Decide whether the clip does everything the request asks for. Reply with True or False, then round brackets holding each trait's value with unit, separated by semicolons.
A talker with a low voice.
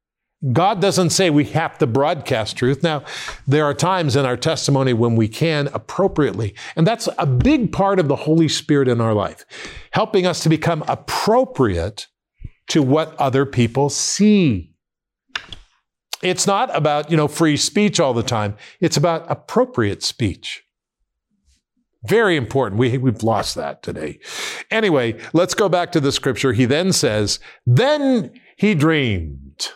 False (150 Hz)